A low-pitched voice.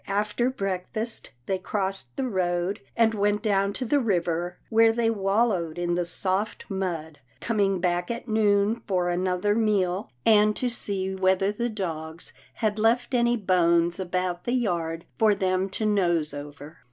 No: high, 195 Hz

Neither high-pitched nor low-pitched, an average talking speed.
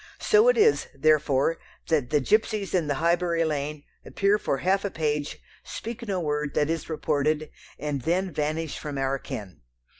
Yes: medium, 155 Hz; average, 170 wpm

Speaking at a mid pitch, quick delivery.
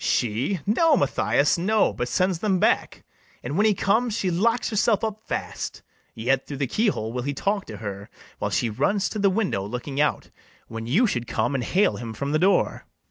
Yes: medium, 155 Hz; fast, 210 wpm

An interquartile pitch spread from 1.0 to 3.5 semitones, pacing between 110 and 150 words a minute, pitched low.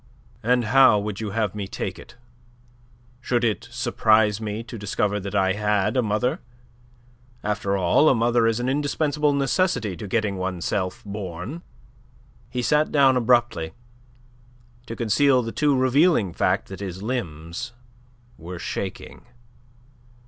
No: average, 4.3 semitones; average, 140 wpm; low, 110 Hz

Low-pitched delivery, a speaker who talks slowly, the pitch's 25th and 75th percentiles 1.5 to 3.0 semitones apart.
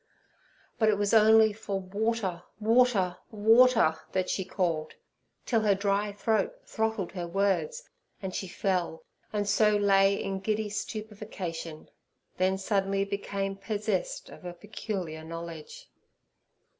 No: high, 200 Hz; slow, 125 wpm; narrow, 2.6 semitones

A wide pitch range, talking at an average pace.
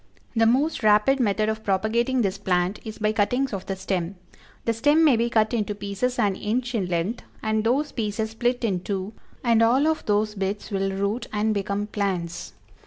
No: average, 2.9 semitones; average, 190 wpm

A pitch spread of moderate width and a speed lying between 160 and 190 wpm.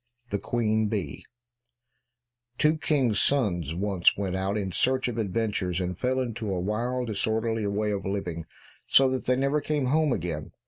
Yes: average, 4.9 semitones; average, 170 wpm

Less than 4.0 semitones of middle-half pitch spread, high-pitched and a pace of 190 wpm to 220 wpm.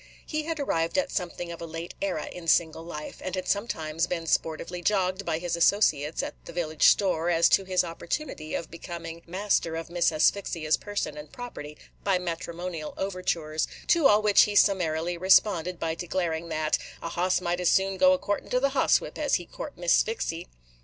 No: average, 2.9 semitones; medium, 175 Hz; average, 195 wpm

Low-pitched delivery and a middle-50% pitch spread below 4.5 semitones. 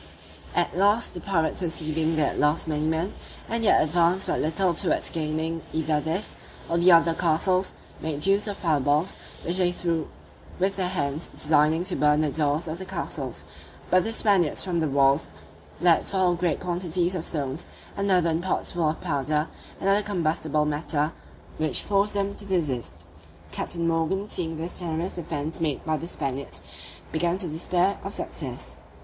No: medium, 165 Hz; average, 2.9 semitones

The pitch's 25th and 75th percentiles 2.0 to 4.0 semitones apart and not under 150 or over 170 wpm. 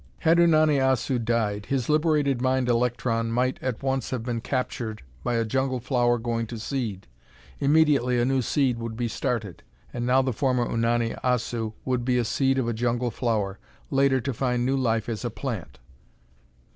No: narrow, 2.4 semitones; average, 180 wpm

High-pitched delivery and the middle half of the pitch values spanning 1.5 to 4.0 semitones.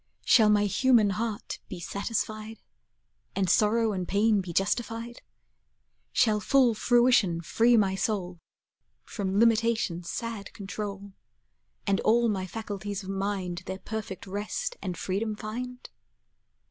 Yes: high, 210 Hz; average, 2.8 semitones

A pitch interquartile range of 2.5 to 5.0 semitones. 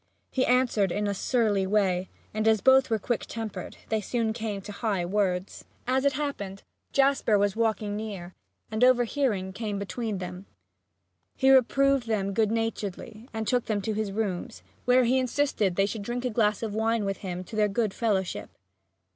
Yes: average, 3.2 semitones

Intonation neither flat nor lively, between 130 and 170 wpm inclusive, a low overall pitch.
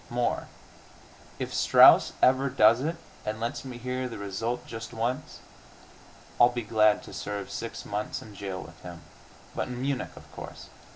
Yes: average, 3.4 semitones; average, 165 wpm; low, 115 Hz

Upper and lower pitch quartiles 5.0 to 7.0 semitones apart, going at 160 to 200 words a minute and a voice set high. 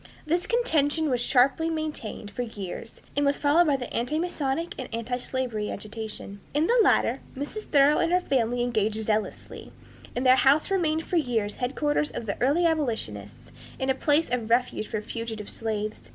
Yes: wide, 5.5 semitones; average, 165 wpm; very high, 255 Hz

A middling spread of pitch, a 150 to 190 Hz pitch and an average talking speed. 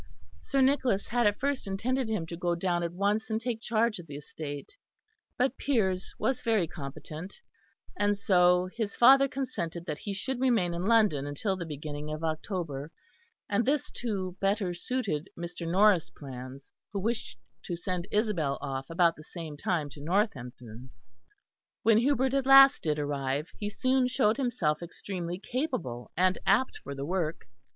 No: wide, 6.6 semitones; medium, 185 Hz; average, 165 wpm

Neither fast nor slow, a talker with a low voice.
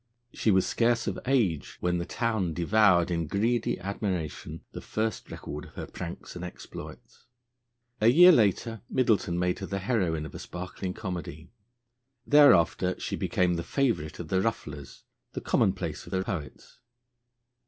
Yes: average, 155 wpm; very low, 95 Hz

